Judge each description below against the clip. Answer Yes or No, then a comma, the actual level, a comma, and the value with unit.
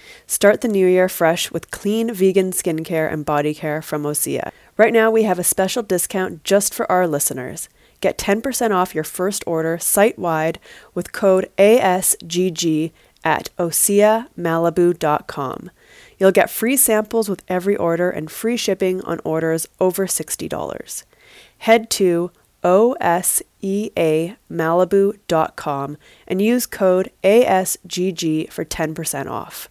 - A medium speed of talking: No, slow, 125 wpm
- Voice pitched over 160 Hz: Yes, medium, 185 Hz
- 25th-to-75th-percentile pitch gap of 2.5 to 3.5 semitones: No, average, 3.9 semitones